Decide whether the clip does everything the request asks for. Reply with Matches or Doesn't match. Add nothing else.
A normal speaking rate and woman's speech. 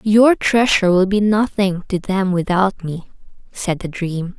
Matches